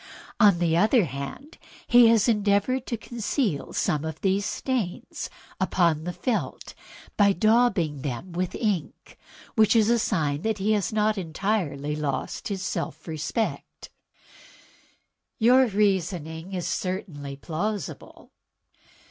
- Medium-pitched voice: No, high, 195 Hz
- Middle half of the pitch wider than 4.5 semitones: Yes, average, 5.3 semitones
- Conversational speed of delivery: No, slow, 120 wpm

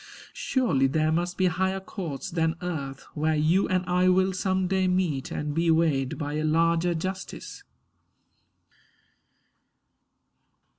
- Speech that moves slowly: Yes, slow, 130 wpm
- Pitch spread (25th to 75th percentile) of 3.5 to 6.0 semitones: No, average, 3.1 semitones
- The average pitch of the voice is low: No, medium, 170 Hz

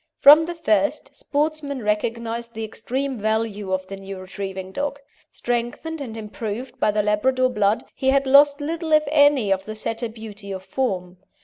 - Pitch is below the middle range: No, high, 230 Hz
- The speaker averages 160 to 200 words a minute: Yes, average, 170 wpm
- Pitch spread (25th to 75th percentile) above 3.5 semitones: Yes, average, 5.3 semitones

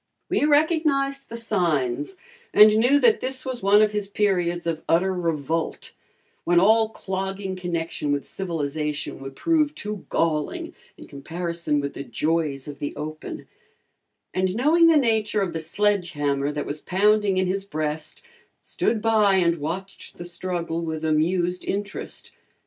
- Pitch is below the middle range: No, medium, 185 Hz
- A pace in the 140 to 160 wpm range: Yes, average, 150 wpm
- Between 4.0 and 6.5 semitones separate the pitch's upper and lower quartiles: Yes, average, 5.1 semitones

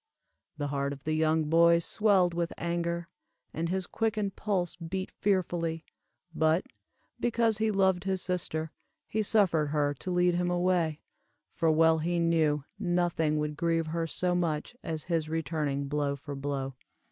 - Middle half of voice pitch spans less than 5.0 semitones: Yes, narrow, 2.6 semitones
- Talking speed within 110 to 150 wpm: No, average, 160 wpm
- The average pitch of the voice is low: No, medium, 170 Hz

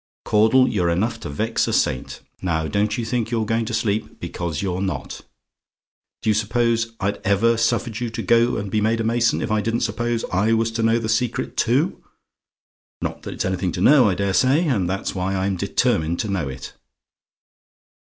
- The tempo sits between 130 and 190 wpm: No, average, 200 wpm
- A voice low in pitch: Yes, low, 110 Hz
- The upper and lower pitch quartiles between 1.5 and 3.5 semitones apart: Yes, average, 3.2 semitones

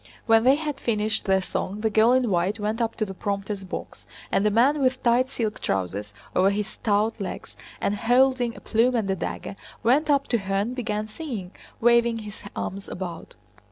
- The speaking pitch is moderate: No, high, 220 Hz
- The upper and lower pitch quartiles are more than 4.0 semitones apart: No, average, 3.6 semitones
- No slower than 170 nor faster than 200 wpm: Yes, average, 195 wpm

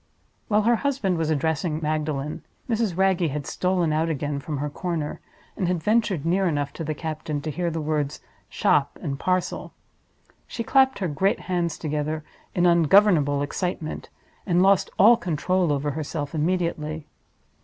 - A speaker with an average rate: Yes, average, 155 wpm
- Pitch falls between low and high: Yes, medium, 165 Hz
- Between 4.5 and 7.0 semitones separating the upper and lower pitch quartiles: No, average, 3.6 semitones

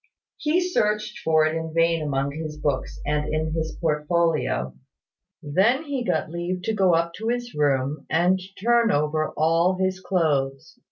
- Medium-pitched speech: Yes, medium, 165 Hz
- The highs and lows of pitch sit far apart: No, average, 3.9 semitones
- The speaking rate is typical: Yes, average, 160 wpm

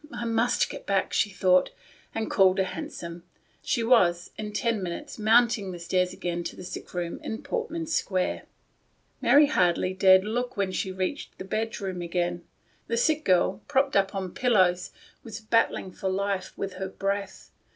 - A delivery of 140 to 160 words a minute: No, average, 170 wpm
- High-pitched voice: Yes, high, 195 Hz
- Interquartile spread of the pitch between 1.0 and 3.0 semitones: No, average, 3.8 semitones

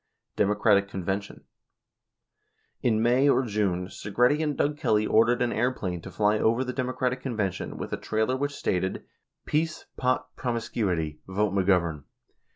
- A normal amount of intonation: Yes, average, 4.6 semitones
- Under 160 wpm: Yes, average, 140 wpm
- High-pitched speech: No, low, 110 Hz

